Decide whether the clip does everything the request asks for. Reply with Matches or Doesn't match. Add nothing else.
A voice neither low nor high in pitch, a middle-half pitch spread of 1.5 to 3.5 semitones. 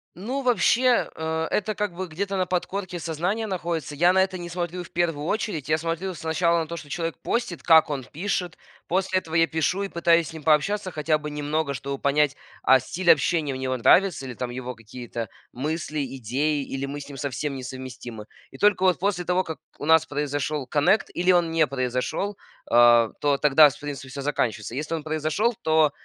Doesn't match